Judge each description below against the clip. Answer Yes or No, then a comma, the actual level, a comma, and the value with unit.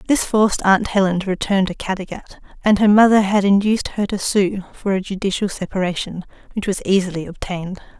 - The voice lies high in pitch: Yes, high, 195 Hz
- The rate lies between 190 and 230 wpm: No, average, 180 wpm